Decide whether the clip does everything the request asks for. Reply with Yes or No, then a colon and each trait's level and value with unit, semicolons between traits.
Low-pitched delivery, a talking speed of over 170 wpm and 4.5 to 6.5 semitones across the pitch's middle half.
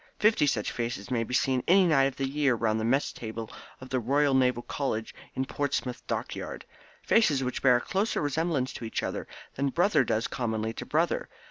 No: low, 130 Hz; average, 200 wpm; average, 3.6 semitones